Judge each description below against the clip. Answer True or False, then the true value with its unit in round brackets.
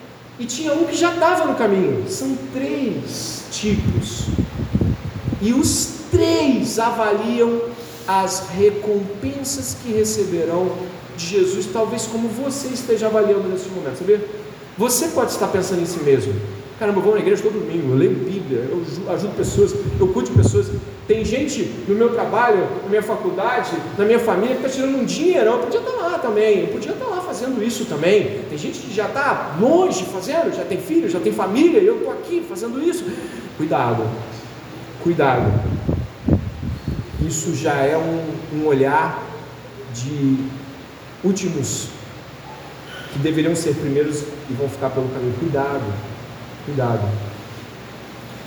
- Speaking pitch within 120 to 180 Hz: False (190 Hz)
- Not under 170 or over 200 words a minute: False (150 wpm)